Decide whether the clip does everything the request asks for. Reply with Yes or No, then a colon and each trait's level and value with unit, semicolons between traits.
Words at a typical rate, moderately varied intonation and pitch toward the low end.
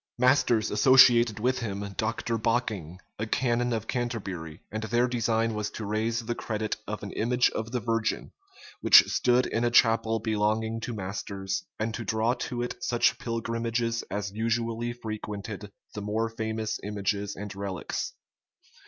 No: average, 155 wpm; narrow, 2.0 semitones; low, 110 Hz